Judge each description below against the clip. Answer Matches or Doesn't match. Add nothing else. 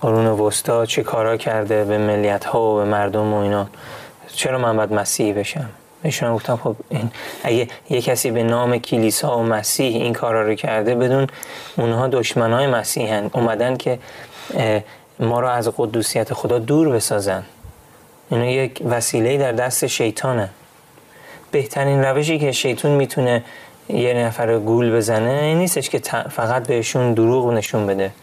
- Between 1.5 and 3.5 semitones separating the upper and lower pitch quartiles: Matches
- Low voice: Matches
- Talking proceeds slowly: Doesn't match